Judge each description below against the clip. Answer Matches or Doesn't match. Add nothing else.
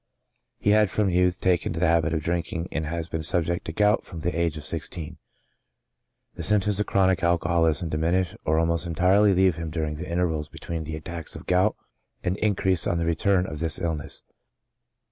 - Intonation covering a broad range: Doesn't match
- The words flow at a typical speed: Matches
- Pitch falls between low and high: Doesn't match